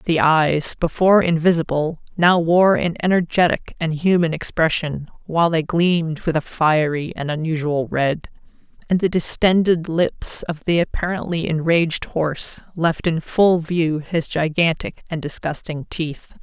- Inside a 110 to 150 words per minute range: Yes, average, 140 wpm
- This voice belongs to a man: No, female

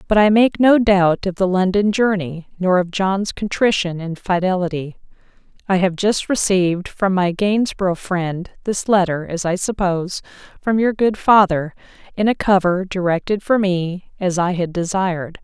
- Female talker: Yes, female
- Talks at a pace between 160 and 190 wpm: Yes, average, 165 wpm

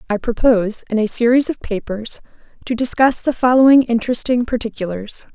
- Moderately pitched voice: No, high, 235 Hz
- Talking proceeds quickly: No, average, 145 wpm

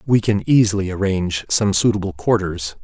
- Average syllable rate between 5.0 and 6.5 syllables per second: Yes, 5.3 syllables/s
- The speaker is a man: Yes, male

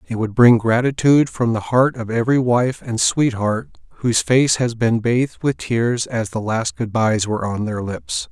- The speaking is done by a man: Yes, male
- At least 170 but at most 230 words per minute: Yes, average, 200 wpm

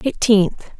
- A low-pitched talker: No, high, 210 Hz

